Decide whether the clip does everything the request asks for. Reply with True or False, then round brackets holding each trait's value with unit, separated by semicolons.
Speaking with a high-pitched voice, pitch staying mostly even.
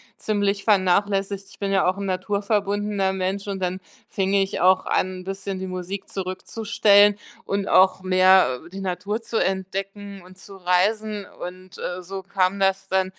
True (195 Hz; 1.3 semitones)